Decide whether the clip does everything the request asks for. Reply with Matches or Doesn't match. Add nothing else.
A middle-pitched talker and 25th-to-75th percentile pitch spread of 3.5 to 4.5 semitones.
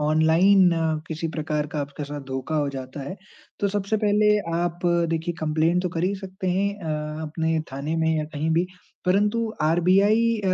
Matches